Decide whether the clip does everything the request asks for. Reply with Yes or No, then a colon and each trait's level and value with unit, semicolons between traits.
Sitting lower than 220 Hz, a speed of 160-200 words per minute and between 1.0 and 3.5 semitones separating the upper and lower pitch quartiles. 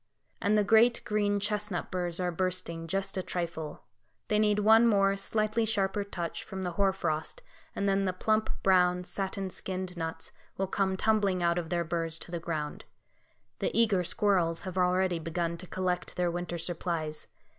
Yes: medium, 185 Hz; average, 175 wpm; average, 2.8 semitones